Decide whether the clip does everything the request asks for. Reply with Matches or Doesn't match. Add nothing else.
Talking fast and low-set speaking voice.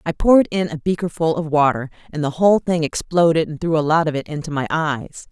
Doesn't match